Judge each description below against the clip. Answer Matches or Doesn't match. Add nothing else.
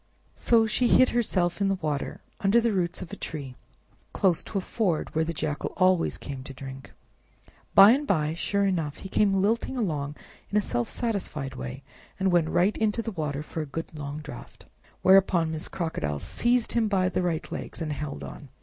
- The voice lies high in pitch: Doesn't match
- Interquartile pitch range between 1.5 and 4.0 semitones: Doesn't match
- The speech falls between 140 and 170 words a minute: Doesn't match